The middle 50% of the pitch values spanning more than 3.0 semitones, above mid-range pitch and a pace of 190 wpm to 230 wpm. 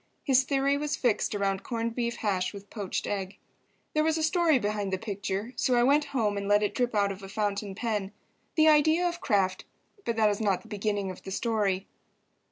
Yes: average, 4.9 semitones; high, 215 Hz; fast, 205 wpm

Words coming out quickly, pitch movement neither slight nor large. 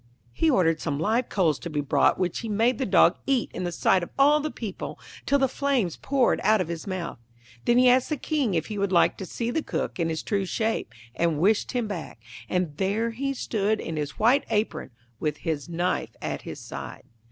No: fast, 220 wpm; wide, 6.4 semitones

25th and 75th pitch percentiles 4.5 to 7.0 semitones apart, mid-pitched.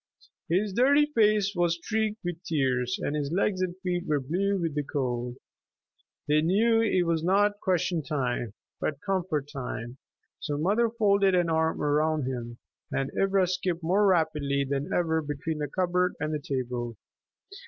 Yes: average, 5.0 semitones; medium, 165 Hz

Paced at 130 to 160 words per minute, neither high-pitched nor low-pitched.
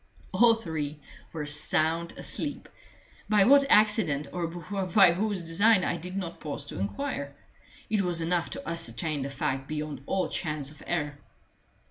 Yes: average, 150 wpm; medium, 165 Hz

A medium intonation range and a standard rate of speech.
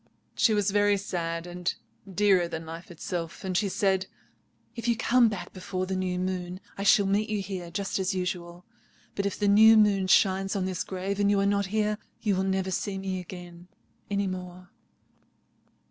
No: narrow, 1.9 semitones; average, 185 wpm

